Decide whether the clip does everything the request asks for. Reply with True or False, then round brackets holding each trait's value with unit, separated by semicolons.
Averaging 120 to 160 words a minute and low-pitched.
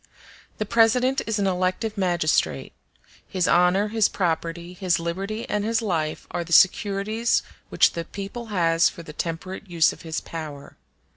False (155 wpm; 185 Hz)